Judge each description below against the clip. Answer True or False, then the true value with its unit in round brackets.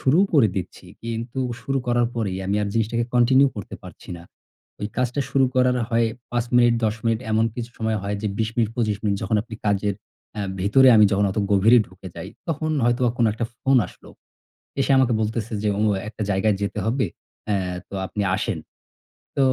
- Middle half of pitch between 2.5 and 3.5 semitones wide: True (2.9 semitones)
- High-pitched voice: False (115 Hz)